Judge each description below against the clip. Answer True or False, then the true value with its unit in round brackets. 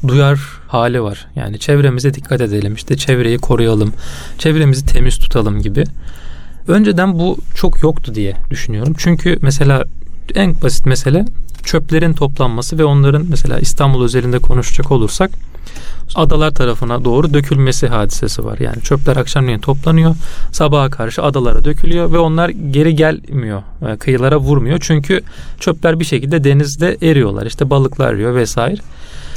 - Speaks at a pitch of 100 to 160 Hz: True (135 Hz)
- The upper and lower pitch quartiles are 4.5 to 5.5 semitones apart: True (4.8 semitones)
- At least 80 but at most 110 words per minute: False (130 wpm)